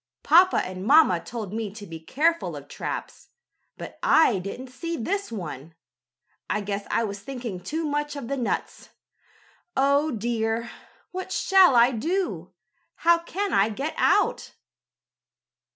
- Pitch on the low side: No, high, 240 Hz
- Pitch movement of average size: No, wide, 7.8 semitones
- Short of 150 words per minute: Yes, average, 140 wpm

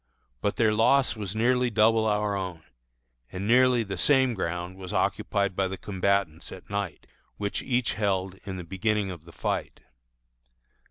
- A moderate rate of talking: Yes, average, 160 wpm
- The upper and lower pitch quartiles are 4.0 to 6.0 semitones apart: No, average, 3.2 semitones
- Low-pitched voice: Yes, low, 100 Hz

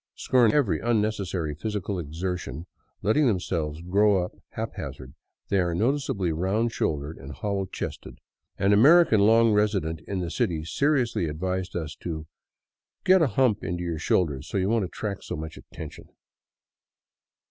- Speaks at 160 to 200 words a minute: No, average, 150 wpm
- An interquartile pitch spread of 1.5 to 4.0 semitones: No, average, 4.8 semitones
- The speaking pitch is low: Yes, very low, 95 Hz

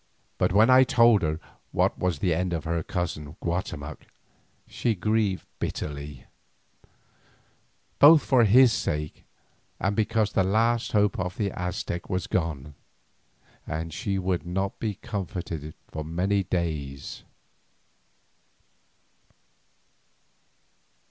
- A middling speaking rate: No, slow, 110 wpm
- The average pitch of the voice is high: No, very low, 90 Hz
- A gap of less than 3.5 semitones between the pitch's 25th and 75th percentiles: No, average, 4.8 semitones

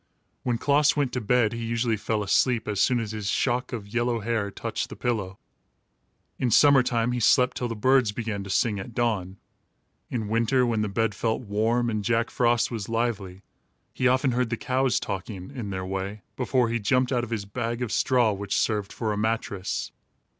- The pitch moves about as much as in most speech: Yes, average, 3.0 semitones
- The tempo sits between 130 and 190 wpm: No, average, 200 wpm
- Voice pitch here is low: Yes, low, 115 Hz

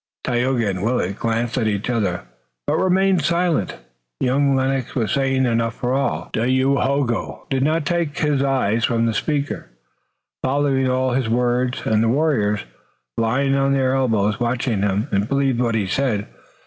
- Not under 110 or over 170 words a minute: Yes, average, 160 wpm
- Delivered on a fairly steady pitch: No, average, 3.3 semitones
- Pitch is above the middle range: No, low, 125 Hz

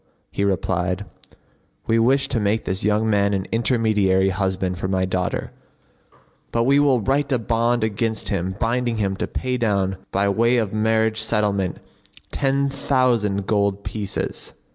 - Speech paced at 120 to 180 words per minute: Yes, average, 150 wpm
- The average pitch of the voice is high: No, low, 105 Hz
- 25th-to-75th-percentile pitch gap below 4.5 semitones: Yes, average, 3.3 semitones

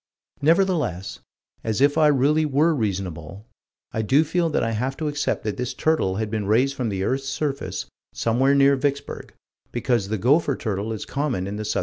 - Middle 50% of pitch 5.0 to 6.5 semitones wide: Yes, average, 5.3 semitones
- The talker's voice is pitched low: Yes, low, 130 Hz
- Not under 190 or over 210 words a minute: Yes, average, 195 wpm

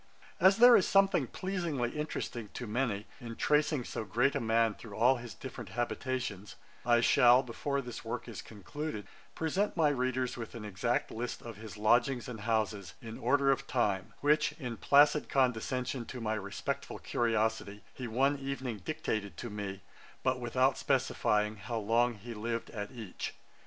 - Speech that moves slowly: No, average, 165 wpm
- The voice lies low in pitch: Yes, low, 120 Hz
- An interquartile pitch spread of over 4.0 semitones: No, average, 3.7 semitones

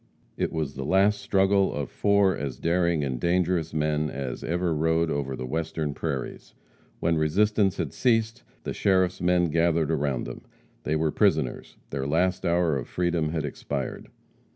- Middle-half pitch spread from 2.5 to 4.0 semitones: Yes, average, 3.7 semitones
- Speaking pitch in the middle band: No, very low, 80 Hz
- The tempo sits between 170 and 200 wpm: No, average, 160 wpm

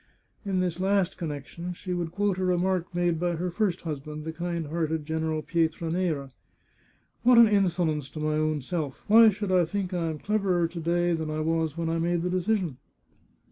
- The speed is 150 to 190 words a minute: No, fast, 205 wpm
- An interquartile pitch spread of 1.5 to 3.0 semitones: Yes, narrow, 2.5 semitones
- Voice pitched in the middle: Yes, medium, 170 Hz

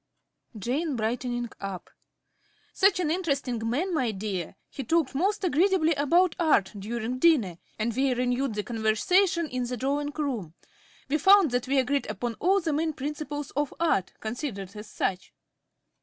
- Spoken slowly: No, average, 155 wpm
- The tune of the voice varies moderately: No, wide, 5.9 semitones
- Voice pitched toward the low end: No, very high, 270 Hz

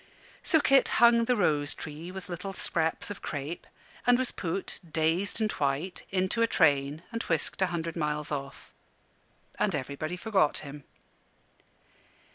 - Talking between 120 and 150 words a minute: Yes, average, 145 wpm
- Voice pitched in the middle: Yes, medium, 170 Hz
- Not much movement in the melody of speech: No, average, 5.2 semitones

